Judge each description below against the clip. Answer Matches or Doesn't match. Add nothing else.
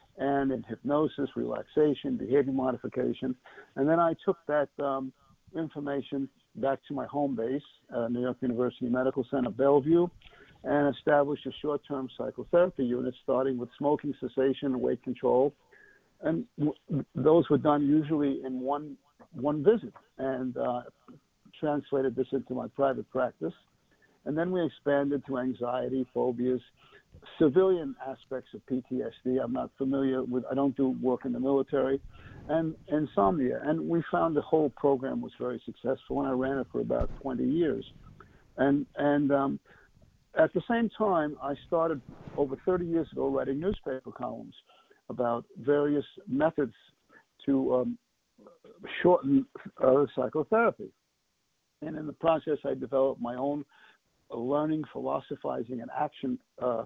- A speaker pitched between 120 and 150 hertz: Matches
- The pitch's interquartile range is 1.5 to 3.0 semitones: Matches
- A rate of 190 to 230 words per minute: Doesn't match